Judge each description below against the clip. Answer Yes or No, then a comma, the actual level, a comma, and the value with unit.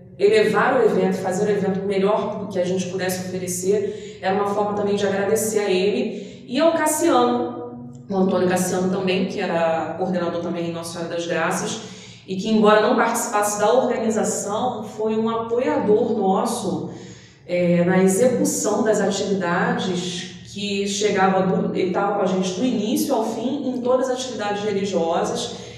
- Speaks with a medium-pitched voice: No, high, 200 Hz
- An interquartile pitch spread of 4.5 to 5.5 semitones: No, average, 2.8 semitones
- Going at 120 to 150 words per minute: No, average, 160 wpm